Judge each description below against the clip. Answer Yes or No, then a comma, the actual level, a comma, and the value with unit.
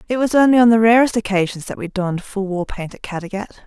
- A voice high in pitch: Yes, high, 210 Hz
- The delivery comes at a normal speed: No, fast, 245 wpm